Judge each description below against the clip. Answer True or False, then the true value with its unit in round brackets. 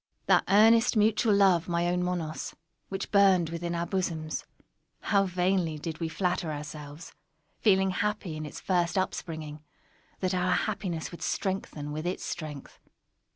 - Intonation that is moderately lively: True (3.3 semitones)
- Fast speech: False (145 wpm)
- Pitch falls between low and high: True (180 Hz)